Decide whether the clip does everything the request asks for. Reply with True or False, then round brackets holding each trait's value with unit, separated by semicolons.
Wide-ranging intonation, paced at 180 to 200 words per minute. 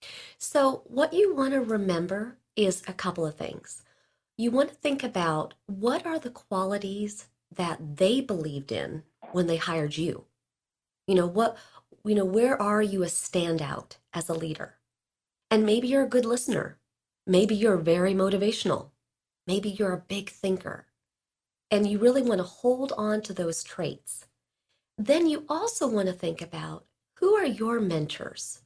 False (5.7 semitones; 160 wpm)